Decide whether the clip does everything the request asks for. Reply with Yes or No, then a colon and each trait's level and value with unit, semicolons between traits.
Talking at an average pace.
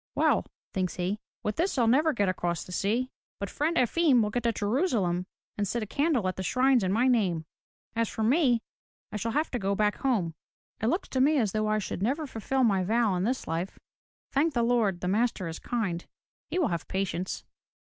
No: fast, 210 wpm